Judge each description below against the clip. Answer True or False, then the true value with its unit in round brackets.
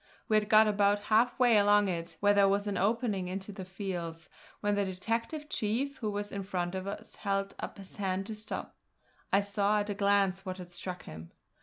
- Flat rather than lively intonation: True (1.9 semitones)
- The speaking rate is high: True (210 wpm)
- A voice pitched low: False (200 Hz)